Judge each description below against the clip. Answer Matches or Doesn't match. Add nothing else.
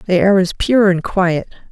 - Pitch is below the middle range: Doesn't match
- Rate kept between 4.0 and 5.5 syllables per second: Matches